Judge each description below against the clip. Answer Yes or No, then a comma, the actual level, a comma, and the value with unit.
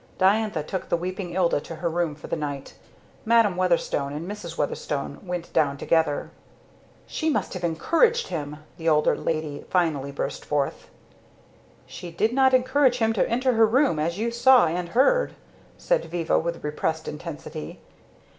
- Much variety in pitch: Yes, wide, 6.4 semitones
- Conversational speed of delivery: Yes, average, 160 wpm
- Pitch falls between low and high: Yes, medium, 175 Hz